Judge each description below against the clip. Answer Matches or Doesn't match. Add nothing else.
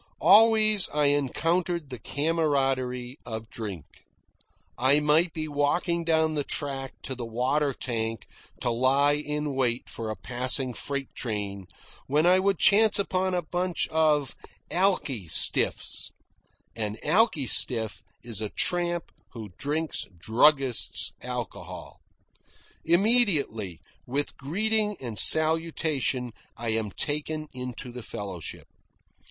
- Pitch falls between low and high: Matches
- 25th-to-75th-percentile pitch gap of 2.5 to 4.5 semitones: Doesn't match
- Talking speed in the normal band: Doesn't match